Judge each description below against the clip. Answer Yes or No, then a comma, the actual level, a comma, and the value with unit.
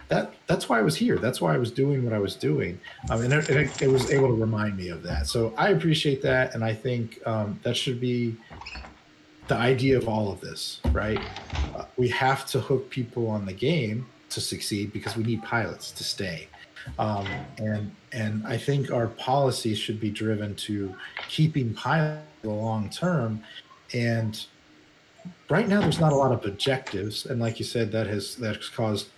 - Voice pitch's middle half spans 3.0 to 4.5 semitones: Yes, average, 4.0 semitones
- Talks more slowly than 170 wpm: No, average, 195 wpm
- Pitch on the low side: Yes, low, 115 Hz